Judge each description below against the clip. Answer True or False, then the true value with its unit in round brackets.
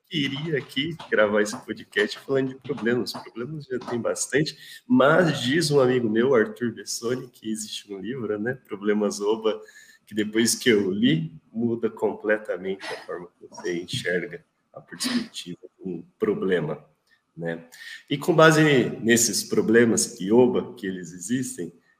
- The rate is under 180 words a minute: True (145 wpm)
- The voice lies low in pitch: True (125 Hz)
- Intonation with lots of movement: True (6.6 semitones)